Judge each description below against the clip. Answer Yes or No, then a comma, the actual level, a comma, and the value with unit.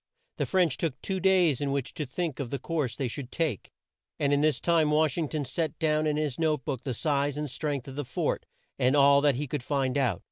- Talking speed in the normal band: No, fast, 245 wpm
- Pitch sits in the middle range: Yes, medium, 145 Hz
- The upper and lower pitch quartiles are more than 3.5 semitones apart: No, average, 2.7 semitones